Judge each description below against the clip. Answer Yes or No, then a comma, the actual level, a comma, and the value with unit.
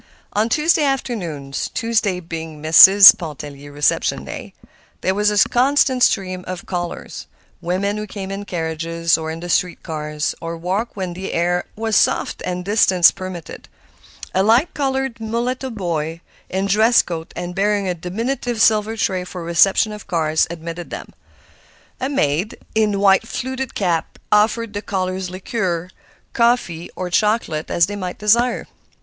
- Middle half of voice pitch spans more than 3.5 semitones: Yes, average, 4.4 semitones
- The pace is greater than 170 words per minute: No, average, 145 wpm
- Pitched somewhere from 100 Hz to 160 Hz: No, high, 190 Hz